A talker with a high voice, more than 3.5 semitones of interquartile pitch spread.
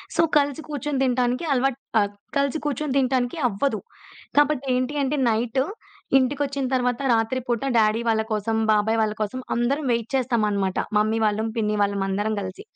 Yes: high, 245 Hz; average, 4.0 semitones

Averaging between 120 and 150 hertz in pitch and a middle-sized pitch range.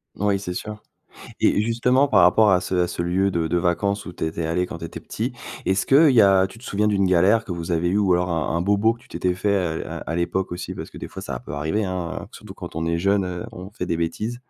No: very low, 95 Hz; average, 3.1 semitones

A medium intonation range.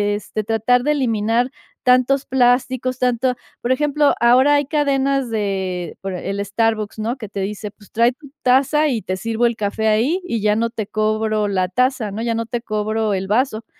Yes: average, 3.3 semitones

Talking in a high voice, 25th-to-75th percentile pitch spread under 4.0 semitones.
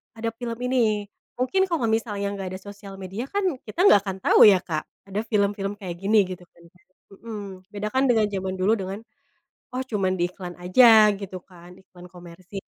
Yes: high, 200 Hz; average, 3.0 semitones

